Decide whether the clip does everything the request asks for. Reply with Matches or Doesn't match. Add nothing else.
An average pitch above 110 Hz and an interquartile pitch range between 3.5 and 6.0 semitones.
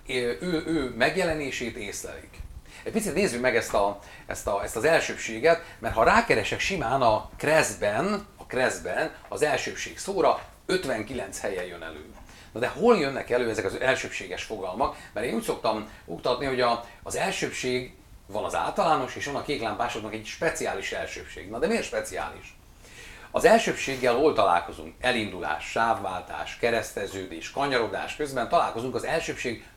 Matches